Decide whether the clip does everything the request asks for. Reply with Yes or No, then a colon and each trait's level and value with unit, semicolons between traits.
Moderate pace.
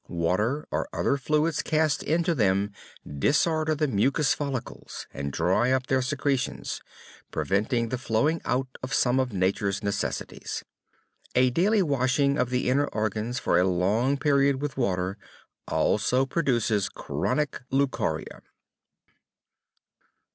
No: slow, 125 wpm